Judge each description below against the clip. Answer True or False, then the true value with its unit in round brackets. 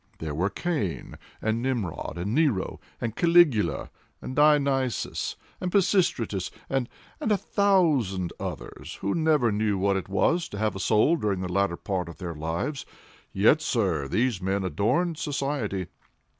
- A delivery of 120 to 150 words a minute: True (145 wpm)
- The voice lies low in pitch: True (110 Hz)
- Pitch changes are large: True (7.7 semitones)